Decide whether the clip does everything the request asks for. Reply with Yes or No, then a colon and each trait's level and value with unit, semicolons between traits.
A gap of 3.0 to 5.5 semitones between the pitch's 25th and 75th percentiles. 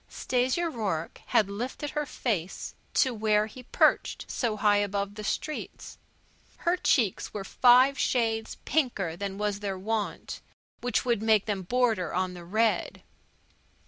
Yes: average, 3.7 semitones